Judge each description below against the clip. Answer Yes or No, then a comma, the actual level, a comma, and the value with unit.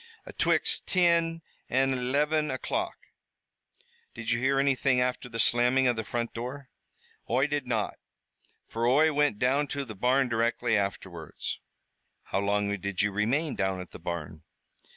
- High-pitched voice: No, low, 125 Hz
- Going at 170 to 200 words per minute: No, average, 150 wpm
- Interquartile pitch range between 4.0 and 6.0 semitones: Yes, average, 4.7 semitones